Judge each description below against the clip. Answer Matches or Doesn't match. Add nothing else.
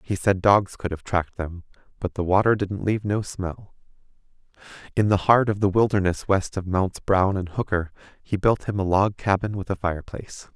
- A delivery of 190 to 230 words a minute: Matches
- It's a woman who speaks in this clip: Doesn't match